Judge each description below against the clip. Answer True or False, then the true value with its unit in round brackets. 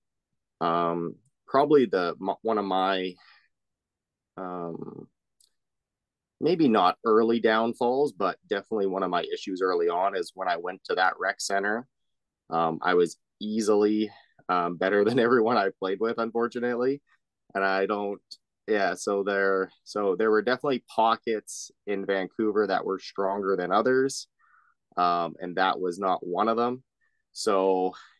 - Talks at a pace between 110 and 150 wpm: True (140 wpm)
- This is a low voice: True (105 Hz)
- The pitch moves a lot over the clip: False (4.0 semitones)